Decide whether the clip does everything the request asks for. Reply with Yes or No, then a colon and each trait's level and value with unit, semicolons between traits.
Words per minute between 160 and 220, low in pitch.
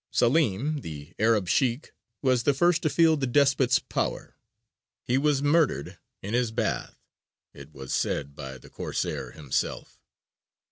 No: average, 140 wpm; low, 125 Hz